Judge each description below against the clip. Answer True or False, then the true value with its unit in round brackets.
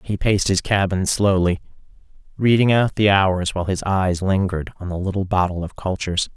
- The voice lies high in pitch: False (95 Hz)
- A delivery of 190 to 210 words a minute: False (180 wpm)